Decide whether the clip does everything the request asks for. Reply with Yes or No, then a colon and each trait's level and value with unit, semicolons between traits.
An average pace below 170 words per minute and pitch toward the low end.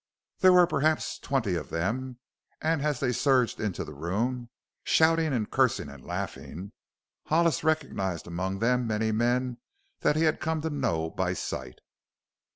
Yes: average, 155 wpm; low, 125 Hz